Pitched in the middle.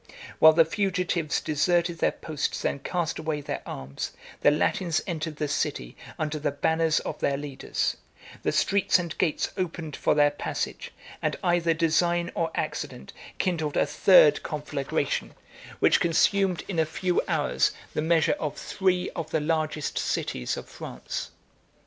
Yes: medium, 160 Hz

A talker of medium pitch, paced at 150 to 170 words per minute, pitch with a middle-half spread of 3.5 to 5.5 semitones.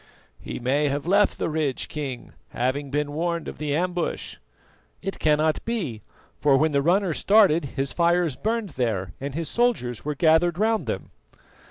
Yes: medium, 155 Hz; average, 165 wpm; average, 4.1 semitones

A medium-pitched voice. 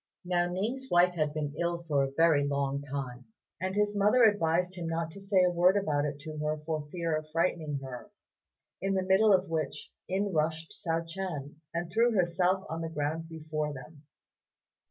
Yes: medium, 165 Hz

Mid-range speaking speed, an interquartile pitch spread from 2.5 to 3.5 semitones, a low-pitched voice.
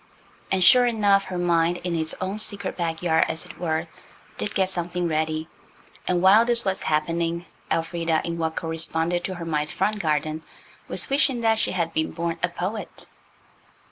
No: average, 170 wpm; average, 2.9 semitones; medium, 170 Hz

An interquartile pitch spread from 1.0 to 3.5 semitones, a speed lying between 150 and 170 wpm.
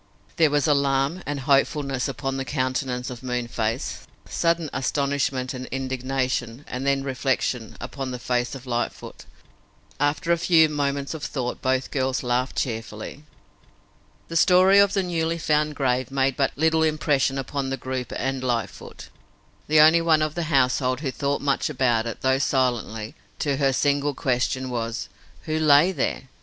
Yes: average, 2.8 semitones; average, 160 wpm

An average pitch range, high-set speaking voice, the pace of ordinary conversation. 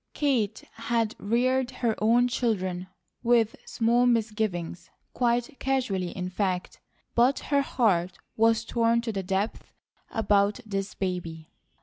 No: average, 3.9 semitones; high, 225 Hz; slow, 120 wpm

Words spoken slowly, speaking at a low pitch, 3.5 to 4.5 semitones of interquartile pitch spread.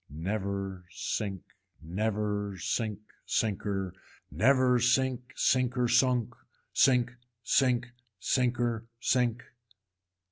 Yes: slow, 75 wpm; low, 115 Hz; average, 4.0 semitones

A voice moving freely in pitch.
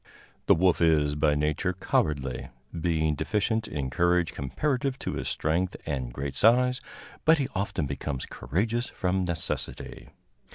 Yes: wide, 6.1 semitones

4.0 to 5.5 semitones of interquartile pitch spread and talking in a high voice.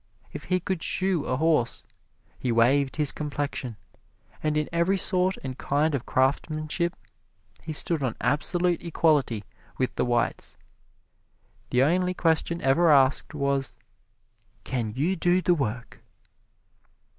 No: average, 4.4 semitones; medium, 150 Hz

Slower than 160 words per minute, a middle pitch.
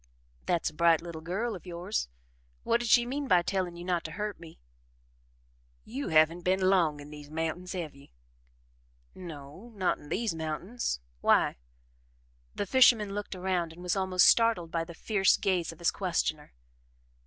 No: average, 165 wpm; medium, 180 Hz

